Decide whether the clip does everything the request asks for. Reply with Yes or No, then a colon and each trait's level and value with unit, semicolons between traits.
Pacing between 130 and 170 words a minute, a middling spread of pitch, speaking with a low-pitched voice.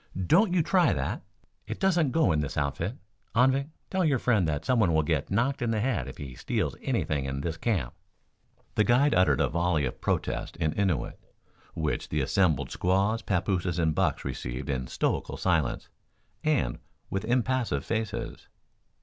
No: average, 165 wpm; wide, 8.5 semitones; very low, 95 Hz